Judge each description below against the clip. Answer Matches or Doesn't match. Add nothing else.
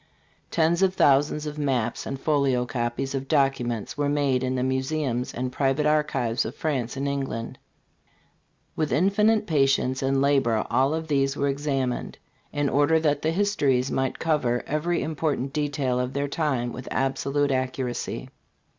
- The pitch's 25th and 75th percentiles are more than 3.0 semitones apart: Doesn't match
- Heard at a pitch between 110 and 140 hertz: Matches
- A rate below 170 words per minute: Matches